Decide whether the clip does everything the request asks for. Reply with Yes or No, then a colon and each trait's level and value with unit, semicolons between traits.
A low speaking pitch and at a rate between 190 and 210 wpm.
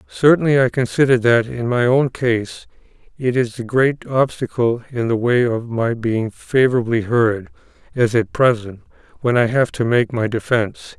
No: low, 120 Hz; average, 170 wpm